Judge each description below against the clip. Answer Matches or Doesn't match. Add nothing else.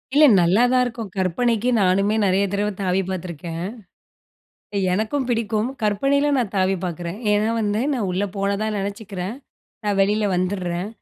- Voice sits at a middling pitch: Doesn't match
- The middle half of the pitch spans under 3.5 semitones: Matches